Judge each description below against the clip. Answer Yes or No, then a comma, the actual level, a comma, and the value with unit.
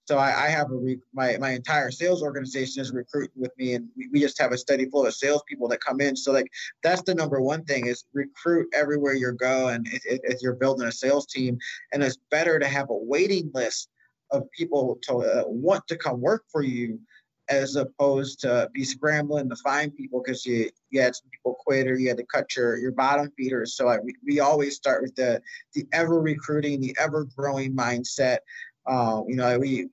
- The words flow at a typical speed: No, fast, 215 wpm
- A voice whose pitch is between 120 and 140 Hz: Yes, low, 135 Hz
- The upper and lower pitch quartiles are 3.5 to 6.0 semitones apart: No, narrow, 2.6 semitones